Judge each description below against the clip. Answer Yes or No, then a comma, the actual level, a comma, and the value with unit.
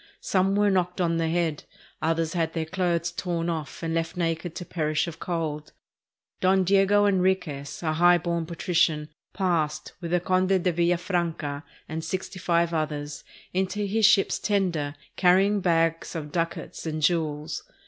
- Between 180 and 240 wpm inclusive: No, average, 160 wpm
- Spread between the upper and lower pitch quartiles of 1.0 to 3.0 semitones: Yes, narrow, 2.4 semitones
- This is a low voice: No, medium, 170 Hz